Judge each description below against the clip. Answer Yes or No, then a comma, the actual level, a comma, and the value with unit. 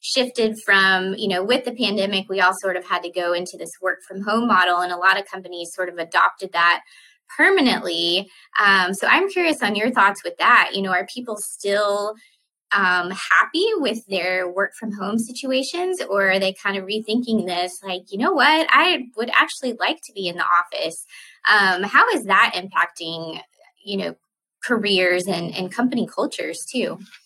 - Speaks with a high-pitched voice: Yes, high, 200 Hz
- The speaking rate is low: No, average, 185 wpm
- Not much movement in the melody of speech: No, average, 4.5 semitones